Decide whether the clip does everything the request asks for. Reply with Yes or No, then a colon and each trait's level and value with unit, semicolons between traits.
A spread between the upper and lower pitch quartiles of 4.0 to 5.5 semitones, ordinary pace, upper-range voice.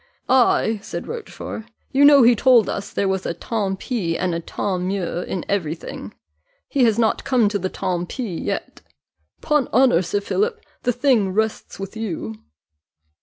Yes: average, 5.1 semitones; average, 170 wpm; high, 210 Hz